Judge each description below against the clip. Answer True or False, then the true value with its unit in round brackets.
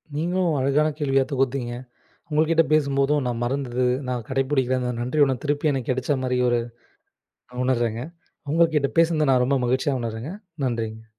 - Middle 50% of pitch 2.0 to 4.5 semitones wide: True (3.1 semitones)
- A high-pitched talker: False (135 Hz)